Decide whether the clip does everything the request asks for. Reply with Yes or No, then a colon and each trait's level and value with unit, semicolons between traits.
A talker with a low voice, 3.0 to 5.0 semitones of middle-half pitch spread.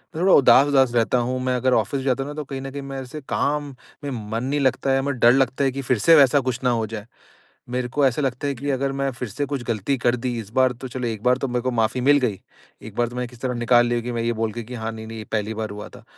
No: low, 125 Hz; narrow, 2.5 semitones